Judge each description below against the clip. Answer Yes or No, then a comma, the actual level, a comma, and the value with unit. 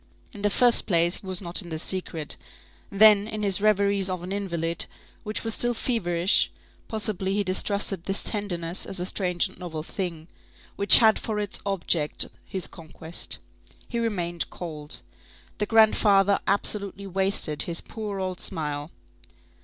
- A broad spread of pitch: No, average, 3.2 semitones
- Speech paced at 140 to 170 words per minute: Yes, average, 155 wpm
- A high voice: Yes, high, 195 Hz